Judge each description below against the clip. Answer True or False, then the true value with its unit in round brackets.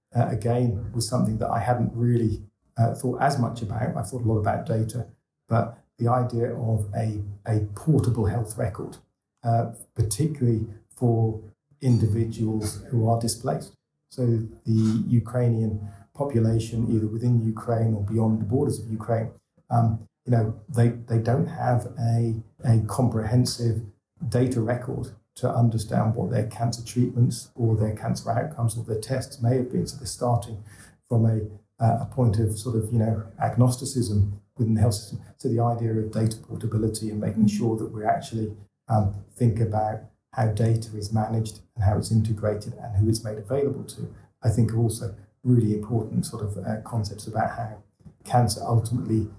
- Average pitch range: False (1.6 semitones)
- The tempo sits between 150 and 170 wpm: True (165 wpm)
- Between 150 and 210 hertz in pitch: False (115 Hz)